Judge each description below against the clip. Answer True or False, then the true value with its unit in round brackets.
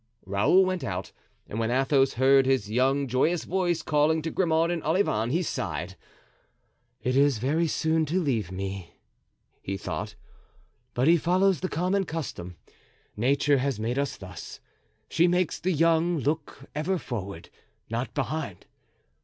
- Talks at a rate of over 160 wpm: False (145 wpm)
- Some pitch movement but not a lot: False (6.1 semitones)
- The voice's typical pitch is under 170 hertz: True (140 Hz)